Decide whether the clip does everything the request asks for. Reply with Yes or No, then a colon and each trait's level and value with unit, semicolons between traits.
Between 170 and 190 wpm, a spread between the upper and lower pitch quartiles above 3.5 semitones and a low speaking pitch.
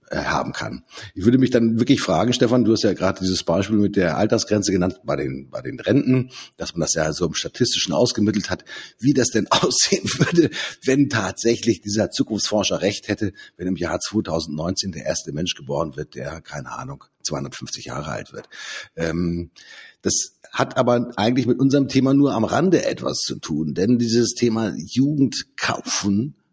Yes: average, 175 wpm; average, 4.8 semitones; low, 110 Hz